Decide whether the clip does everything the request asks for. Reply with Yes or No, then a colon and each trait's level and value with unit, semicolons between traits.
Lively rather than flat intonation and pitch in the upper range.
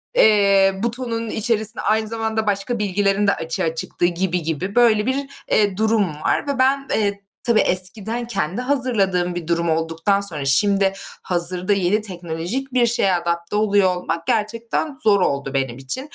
No: average, 4.3 semitones; high, 200 Hz